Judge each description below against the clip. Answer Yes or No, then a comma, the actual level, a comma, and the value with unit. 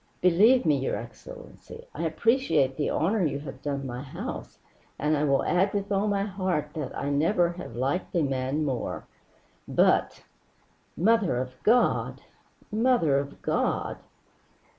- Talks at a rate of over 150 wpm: No, average, 145 wpm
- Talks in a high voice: No, medium, 160 Hz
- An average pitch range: No, wide, 6.4 semitones